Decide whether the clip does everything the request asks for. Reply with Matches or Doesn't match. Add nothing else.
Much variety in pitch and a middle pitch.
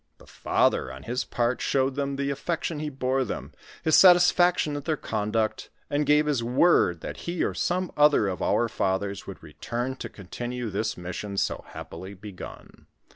Doesn't match